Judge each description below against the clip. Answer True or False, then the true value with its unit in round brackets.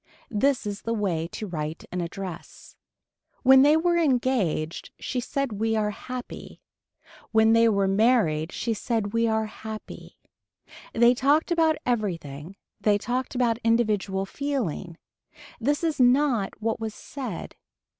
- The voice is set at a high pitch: True (225 Hz)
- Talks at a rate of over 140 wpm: False (135 wpm)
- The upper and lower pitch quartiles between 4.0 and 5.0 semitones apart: True (4.6 semitones)